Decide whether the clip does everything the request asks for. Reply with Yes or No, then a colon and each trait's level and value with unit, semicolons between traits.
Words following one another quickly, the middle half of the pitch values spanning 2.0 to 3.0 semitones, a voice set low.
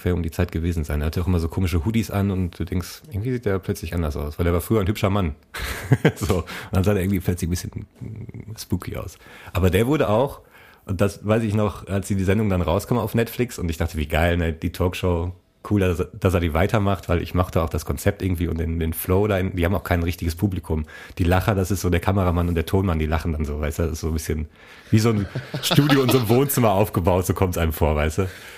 No: fast, 265 wpm; average, 3.8 semitones; very low, 95 Hz